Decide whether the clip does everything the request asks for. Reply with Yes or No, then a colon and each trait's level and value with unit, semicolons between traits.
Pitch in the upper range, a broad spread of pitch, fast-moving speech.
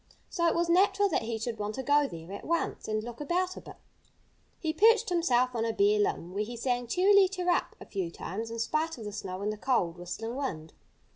Yes: high, 240 Hz; wide, 8.2 semitones; fast, 230 wpm